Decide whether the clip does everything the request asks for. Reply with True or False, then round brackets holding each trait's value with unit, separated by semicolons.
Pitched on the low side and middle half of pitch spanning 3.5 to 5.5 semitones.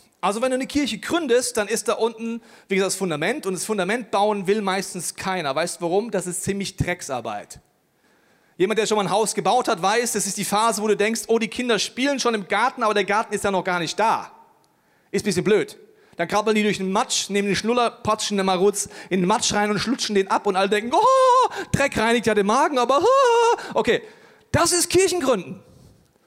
False (215 Hz; 4.2 semitones)